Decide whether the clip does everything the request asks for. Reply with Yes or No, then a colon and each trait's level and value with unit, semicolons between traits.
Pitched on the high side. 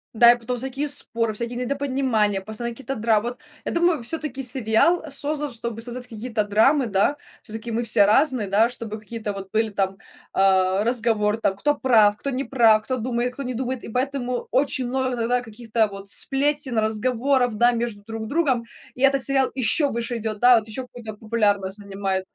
Yes: high, 235 Hz